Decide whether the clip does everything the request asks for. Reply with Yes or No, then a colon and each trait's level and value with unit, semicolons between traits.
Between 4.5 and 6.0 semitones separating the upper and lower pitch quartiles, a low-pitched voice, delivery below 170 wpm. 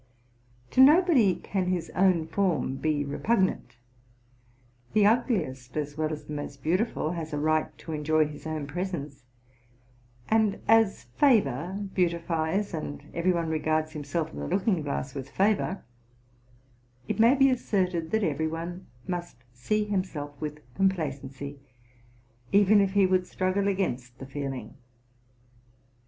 No: average, 4.8 semitones; medium, 170 Hz; slow, 135 wpm